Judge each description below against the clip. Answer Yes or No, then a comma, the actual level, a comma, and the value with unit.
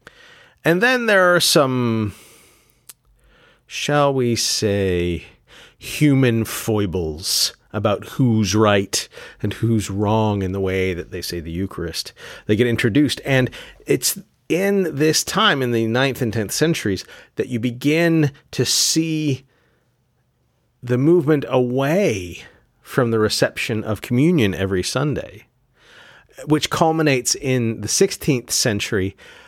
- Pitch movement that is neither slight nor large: No, wide, 6.3 semitones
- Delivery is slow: Yes, slow, 120 wpm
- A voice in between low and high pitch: No, low, 120 Hz